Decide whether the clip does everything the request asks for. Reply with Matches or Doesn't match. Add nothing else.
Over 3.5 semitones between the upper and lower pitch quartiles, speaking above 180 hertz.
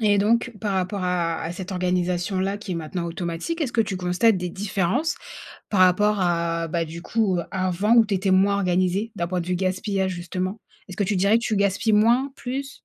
Doesn't match